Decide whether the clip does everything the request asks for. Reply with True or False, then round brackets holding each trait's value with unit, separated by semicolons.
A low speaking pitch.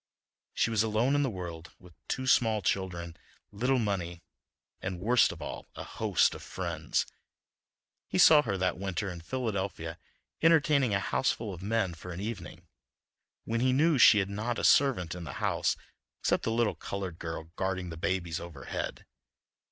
True (100 Hz)